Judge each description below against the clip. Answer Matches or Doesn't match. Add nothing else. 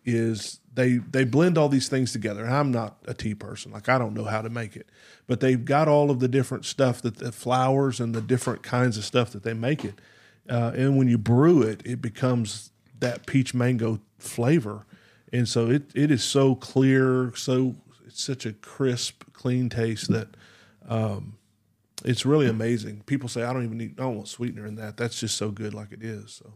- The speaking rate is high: Matches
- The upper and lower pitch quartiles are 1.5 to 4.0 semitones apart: Matches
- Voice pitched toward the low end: Matches